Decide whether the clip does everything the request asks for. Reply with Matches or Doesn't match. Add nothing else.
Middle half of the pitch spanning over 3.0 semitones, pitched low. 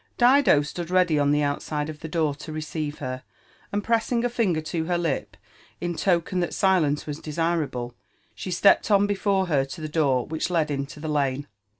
Doesn't match